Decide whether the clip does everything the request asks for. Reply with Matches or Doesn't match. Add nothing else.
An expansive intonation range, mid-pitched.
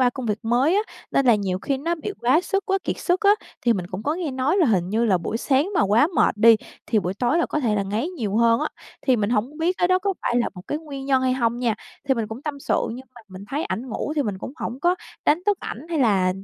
Doesn't match